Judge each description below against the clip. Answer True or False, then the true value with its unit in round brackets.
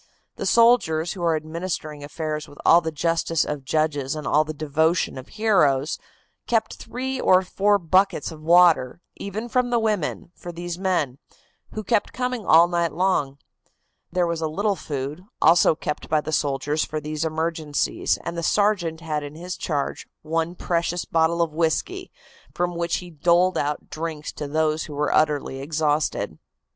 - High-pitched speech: False (165 Hz)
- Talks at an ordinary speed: True (170 wpm)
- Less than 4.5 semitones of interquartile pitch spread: True (2.9 semitones)